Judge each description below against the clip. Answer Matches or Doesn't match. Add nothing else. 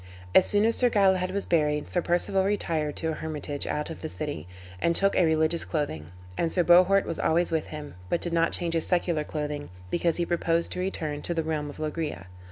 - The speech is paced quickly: Matches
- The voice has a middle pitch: Matches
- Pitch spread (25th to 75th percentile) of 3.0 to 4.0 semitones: Doesn't match